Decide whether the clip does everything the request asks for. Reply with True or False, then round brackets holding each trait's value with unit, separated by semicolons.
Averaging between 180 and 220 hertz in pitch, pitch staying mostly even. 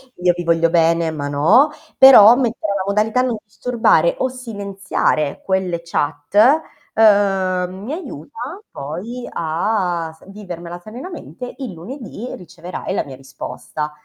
False (190 Hz; 5.9 semitones)